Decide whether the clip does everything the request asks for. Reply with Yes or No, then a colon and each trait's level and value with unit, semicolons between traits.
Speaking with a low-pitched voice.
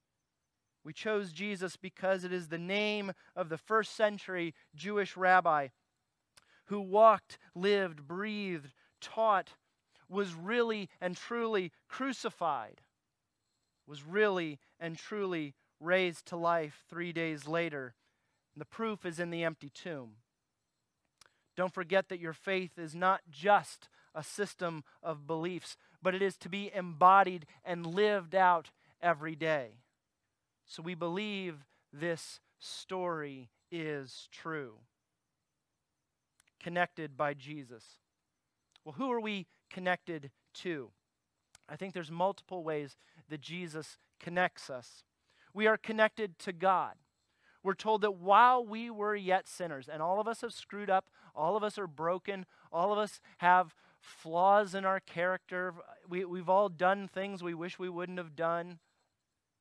No: medium, 180 Hz